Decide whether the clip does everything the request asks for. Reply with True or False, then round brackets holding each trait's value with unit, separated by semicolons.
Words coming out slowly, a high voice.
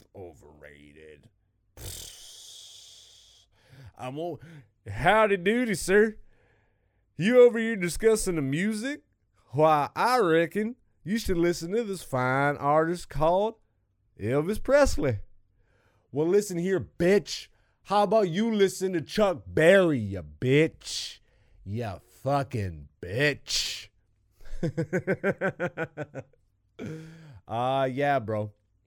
False (90 wpm; 140 Hz)